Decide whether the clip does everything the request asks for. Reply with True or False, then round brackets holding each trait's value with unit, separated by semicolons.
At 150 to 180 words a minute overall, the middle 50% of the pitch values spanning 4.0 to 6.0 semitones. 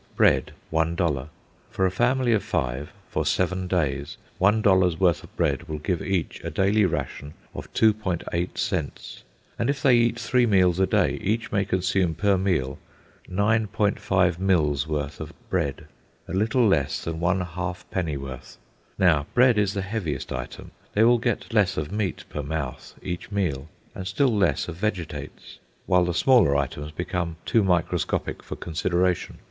True (160 wpm; 4.3 semitones)